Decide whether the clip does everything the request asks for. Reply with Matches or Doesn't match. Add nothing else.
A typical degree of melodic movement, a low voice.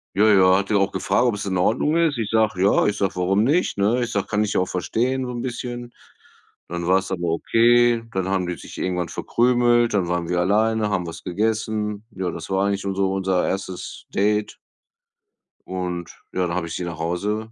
Matches